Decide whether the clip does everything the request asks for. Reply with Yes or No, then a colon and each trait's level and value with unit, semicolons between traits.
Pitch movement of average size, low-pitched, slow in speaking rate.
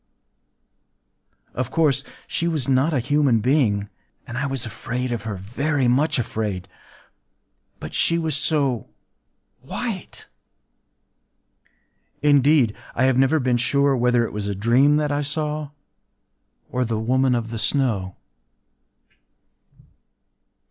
Yes: average, 3.8 semitones; low, 130 Hz; slow, 115 wpm